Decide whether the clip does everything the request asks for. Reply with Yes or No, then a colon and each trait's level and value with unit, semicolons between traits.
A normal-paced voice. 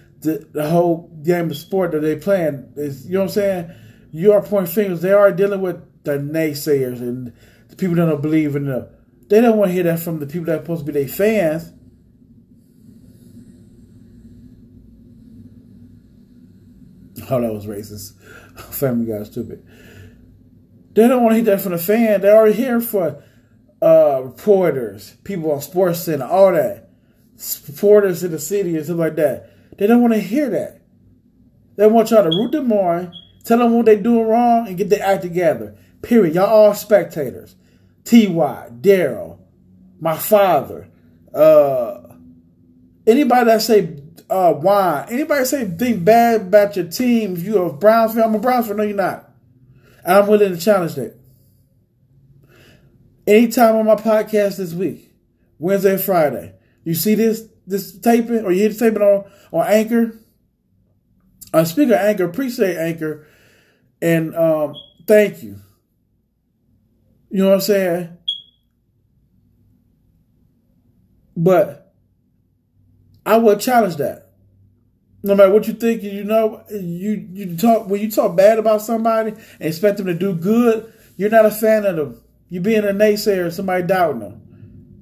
Yes: average, 160 wpm